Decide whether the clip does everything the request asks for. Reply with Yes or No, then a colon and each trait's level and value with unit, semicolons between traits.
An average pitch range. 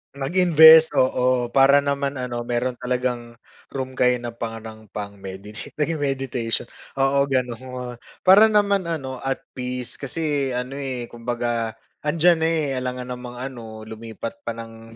Yes: average, 3.0 semitones